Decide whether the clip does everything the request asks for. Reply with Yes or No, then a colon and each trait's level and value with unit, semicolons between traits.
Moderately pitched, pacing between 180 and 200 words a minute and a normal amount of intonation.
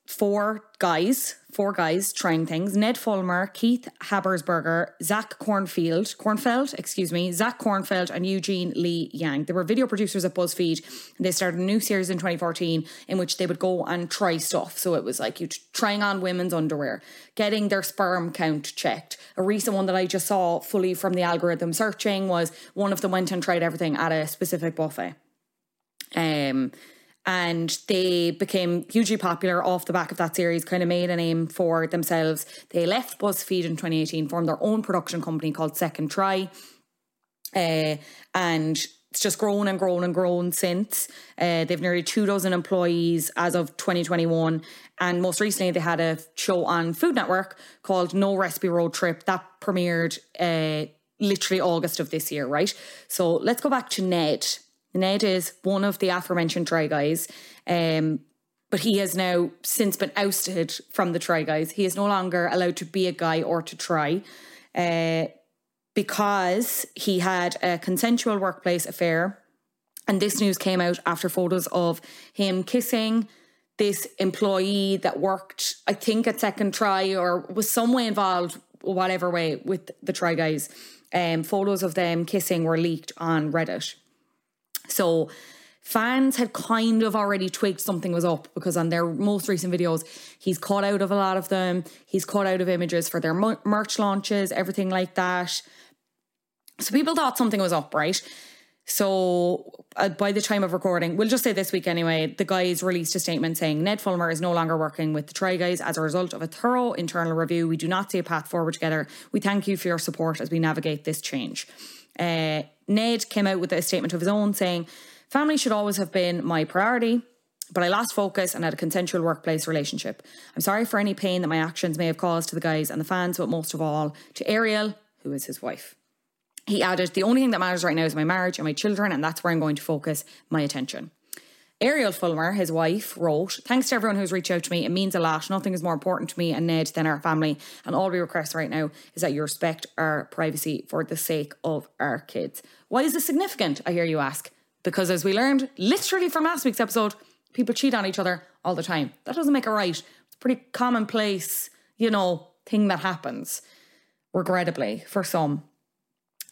Yes: medium, 180 Hz; average, 195 wpm; average, 3.2 semitones